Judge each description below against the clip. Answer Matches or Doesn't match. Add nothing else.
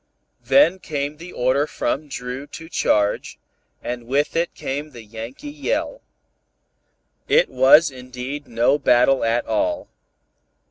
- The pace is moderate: Doesn't match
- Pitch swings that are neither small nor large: Matches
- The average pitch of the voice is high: Doesn't match